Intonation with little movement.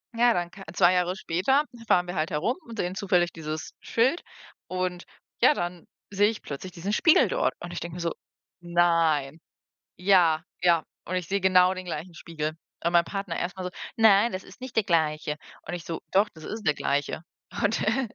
No: average, 3.1 semitones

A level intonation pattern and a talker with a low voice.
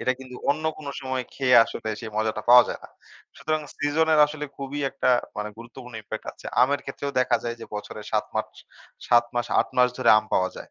No: average, 3.4 semitones; low, 125 Hz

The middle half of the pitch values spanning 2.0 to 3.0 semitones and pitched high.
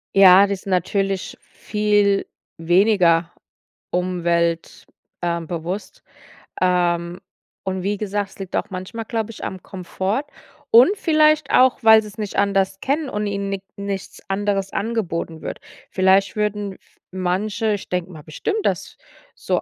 Yes: narrow, 2.6 semitones; high, 195 Hz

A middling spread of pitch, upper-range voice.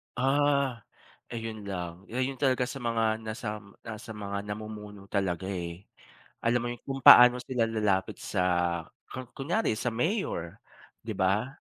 No: average, 3.8 semitones; low, 110 Hz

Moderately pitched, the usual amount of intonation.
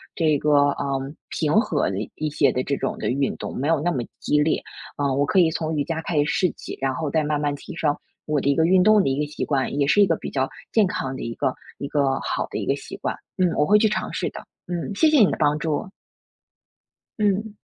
Yes: medium, 150 Hz; average, 3.8 semitones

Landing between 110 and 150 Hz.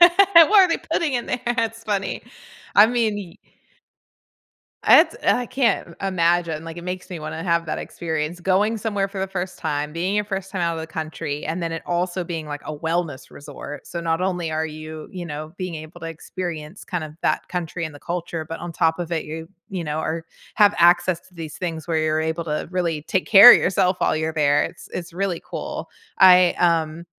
No: medium, 170 Hz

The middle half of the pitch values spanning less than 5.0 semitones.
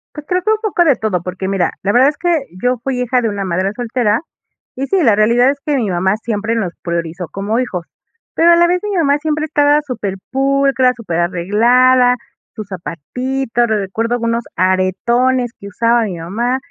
No: wide, 5.4 semitones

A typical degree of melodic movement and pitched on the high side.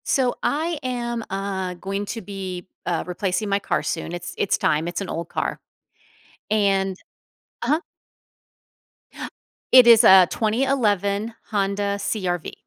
Yes: average, 3.7 semitones; high, 200 Hz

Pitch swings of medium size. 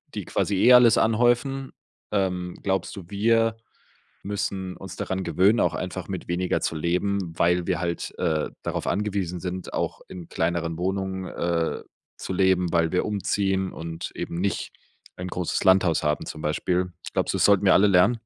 No: narrow, 2.3 semitones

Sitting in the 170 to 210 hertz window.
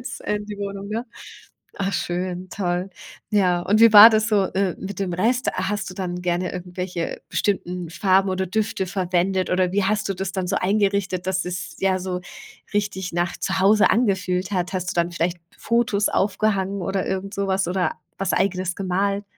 Yes: high, 190 Hz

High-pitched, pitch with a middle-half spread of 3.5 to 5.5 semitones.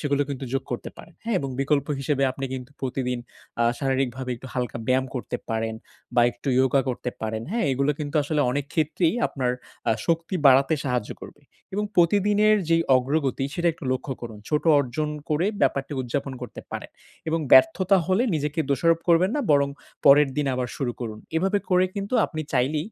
No: medium, 140 Hz; average, 4.3 semitones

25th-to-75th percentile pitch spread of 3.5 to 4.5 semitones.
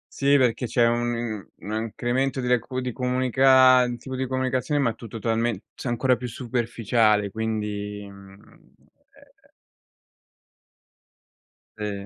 No: average, 2.8 semitones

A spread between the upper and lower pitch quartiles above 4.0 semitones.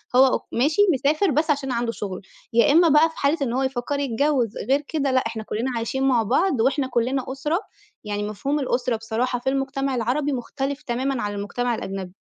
No: average, 3.3 semitones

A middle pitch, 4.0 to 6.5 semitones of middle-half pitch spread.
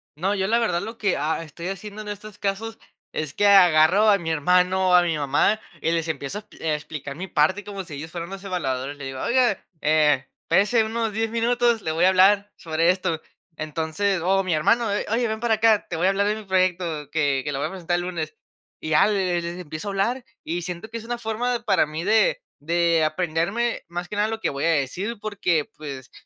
Yes: medium, 180 Hz; average, 4.9 semitones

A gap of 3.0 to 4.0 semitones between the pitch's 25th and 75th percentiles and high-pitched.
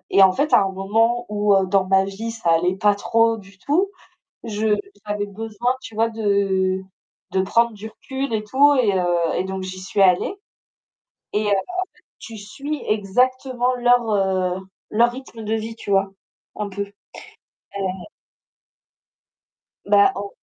Yes: average, 3.4 semitones; high, 210 Hz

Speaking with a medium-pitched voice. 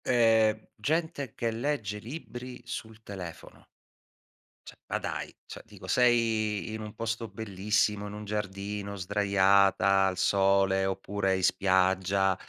No: low, 105 Hz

